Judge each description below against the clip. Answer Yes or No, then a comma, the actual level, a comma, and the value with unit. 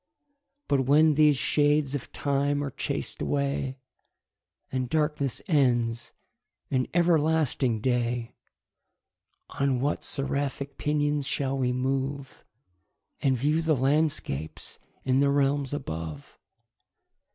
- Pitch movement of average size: No, narrow, 2.3 semitones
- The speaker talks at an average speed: No, slow, 105 wpm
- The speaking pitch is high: No, medium, 140 Hz